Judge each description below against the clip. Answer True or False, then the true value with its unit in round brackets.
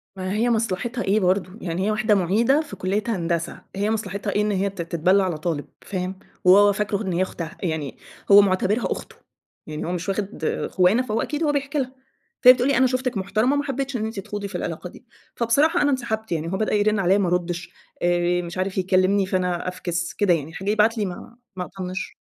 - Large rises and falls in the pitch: False (3.6 semitones)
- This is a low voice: False (195 Hz)